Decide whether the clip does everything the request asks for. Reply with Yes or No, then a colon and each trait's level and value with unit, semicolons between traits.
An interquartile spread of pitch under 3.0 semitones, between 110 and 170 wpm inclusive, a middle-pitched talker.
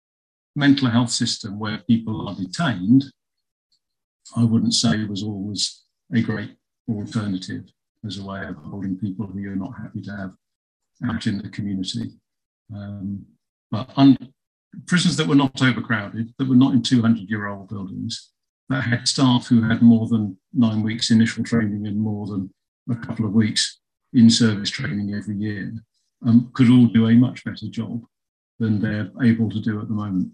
No: narrow, 2.6 semitones; average, 165 wpm; low, 110 Hz